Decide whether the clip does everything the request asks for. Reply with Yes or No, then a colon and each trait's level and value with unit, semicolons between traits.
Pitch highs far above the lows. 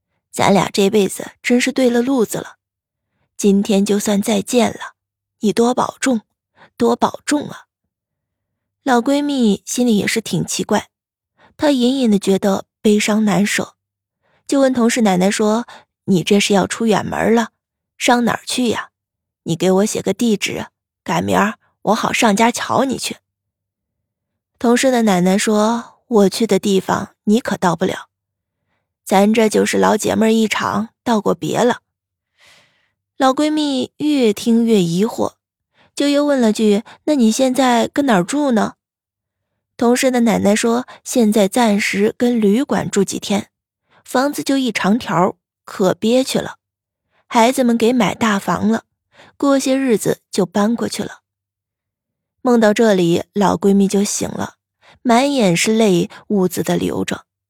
No: average, 4.9 semitones